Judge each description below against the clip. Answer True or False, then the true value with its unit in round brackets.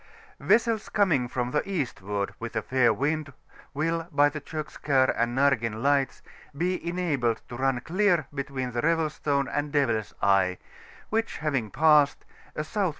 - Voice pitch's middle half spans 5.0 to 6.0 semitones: False (4.6 semitones)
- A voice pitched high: False (140 Hz)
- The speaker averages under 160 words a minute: True (150 wpm)